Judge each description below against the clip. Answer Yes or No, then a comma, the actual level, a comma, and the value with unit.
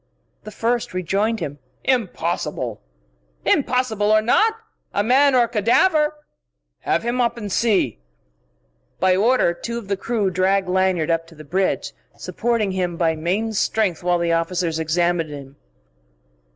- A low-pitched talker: No, high, 195 Hz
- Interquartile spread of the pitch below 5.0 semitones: No, average, 5.3 semitones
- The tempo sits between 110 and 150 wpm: Yes, average, 145 wpm